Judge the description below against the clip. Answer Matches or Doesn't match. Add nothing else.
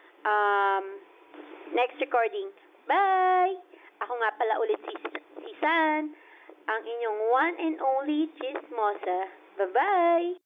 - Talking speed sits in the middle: Doesn't match